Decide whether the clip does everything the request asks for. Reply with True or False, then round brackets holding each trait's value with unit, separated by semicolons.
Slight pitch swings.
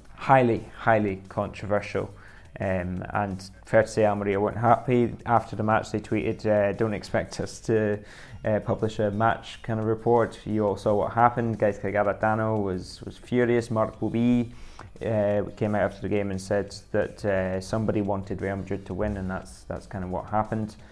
True (2.1 semitones)